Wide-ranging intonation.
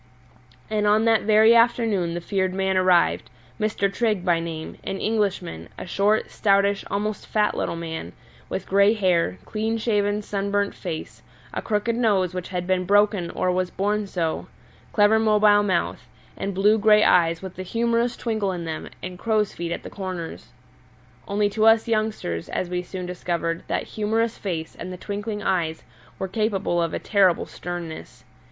No: average, 3.2 semitones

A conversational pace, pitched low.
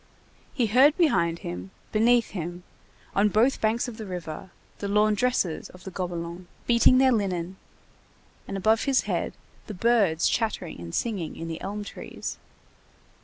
No: average, 150 wpm; high, 205 Hz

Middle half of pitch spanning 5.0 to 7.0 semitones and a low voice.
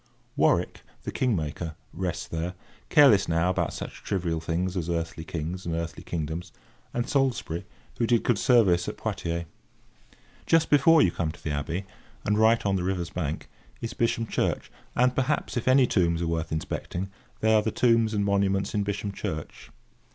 Yes: wide, 5.4 semitones; very low, 95 Hz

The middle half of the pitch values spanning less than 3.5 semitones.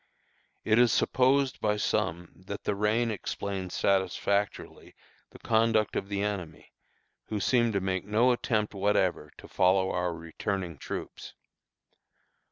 Yes: average, 2.7 semitones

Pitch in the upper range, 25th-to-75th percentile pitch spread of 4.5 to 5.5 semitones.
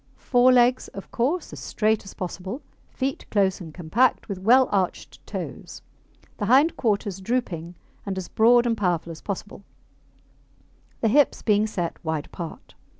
Yes: high, 205 Hz; average, 5.1 semitones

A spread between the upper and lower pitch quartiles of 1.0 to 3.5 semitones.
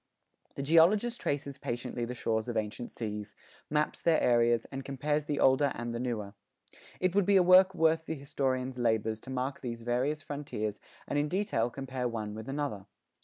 No: average, 4.3 semitones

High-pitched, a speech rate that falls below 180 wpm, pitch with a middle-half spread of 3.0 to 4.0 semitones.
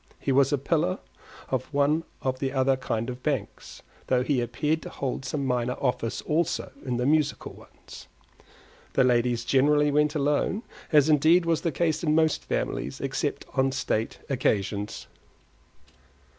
No: low, 135 Hz; average, 155 wpm; average, 3.3 semitones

